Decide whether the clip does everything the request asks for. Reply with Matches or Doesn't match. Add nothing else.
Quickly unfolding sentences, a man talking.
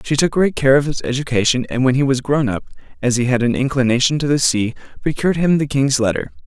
Matches